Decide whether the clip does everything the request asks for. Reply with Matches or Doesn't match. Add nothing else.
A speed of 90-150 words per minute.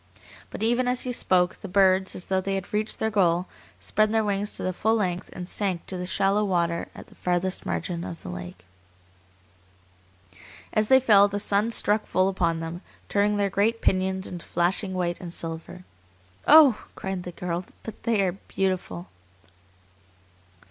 Doesn't match